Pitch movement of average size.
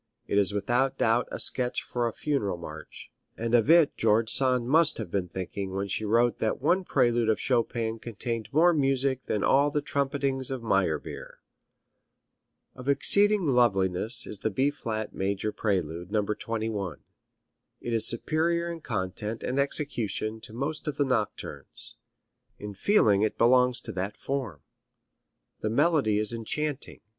Yes: average, 4.8 semitones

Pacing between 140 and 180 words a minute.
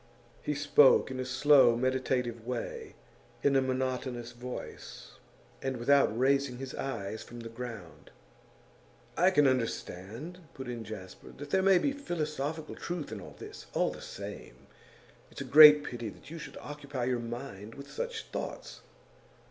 Yes: average, 155 wpm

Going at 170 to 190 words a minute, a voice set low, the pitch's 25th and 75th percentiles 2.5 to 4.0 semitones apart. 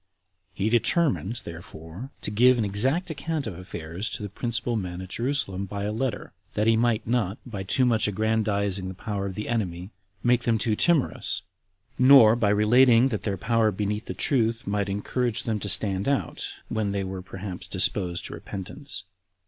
Yes: average, 180 wpm; low, 105 Hz; average, 3.6 semitones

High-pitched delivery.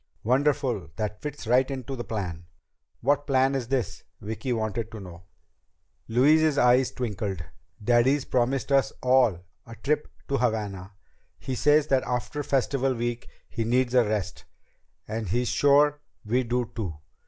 No: low, 125 Hz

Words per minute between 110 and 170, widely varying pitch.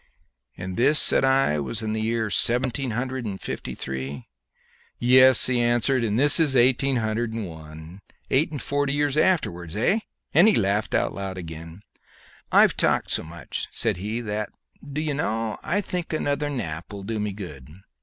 Yes: average, 165 wpm; wide, 6.1 semitones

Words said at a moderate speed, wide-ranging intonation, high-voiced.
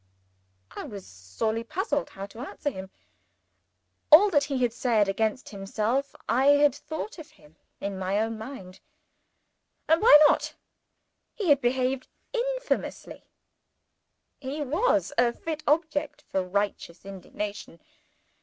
No: slow, 125 wpm; wide, 6.7 semitones; very high, 255 Hz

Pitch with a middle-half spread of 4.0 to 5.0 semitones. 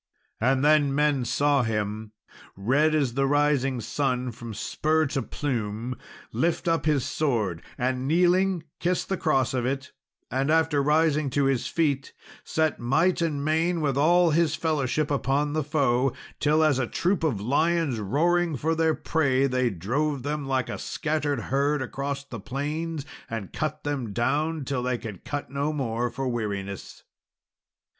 No: average, 3.6 semitones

